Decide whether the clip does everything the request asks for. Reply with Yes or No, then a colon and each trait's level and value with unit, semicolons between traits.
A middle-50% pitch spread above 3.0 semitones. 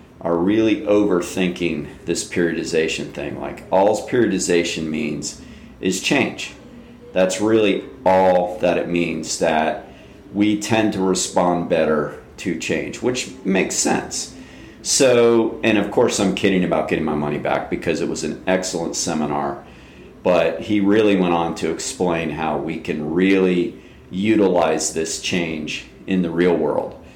Yes: average, 3.7 semitones